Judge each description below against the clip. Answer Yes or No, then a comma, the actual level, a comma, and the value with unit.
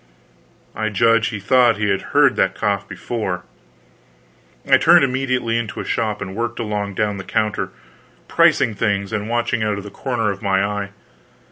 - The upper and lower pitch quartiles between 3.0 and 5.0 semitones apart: No, narrow, 2.4 semitones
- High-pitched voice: No, low, 105 Hz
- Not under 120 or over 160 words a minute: No, average, 170 wpm